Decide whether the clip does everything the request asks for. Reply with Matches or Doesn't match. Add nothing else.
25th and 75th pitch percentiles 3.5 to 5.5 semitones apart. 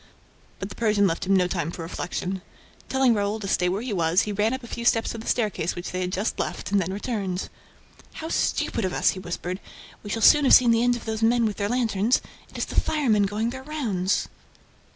Matches